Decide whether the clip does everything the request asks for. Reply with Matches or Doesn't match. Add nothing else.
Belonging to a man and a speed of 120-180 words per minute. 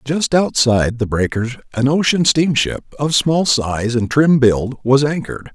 Matches